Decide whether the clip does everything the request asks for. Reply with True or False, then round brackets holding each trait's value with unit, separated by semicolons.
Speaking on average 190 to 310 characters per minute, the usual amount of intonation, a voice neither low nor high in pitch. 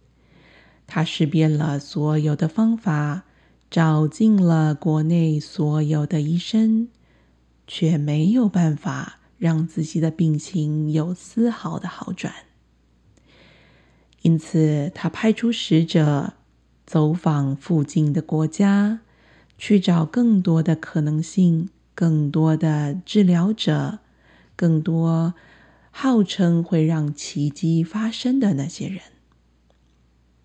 False (155 characters per minute; 3.3 semitones; 160 Hz)